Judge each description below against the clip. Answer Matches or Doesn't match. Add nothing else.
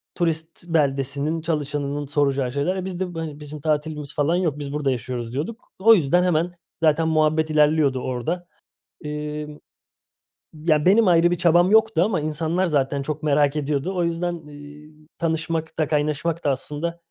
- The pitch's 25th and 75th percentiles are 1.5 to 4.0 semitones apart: Matches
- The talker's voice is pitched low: Doesn't match